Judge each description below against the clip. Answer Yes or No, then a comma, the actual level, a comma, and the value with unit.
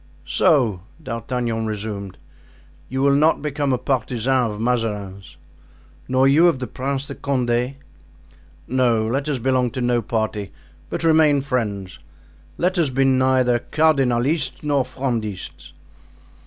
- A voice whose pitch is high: No, low, 130 Hz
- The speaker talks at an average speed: No, slow, 130 wpm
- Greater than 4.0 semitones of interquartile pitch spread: No, average, 3.4 semitones